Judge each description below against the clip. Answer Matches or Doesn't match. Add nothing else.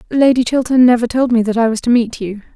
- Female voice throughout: Matches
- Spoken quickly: Matches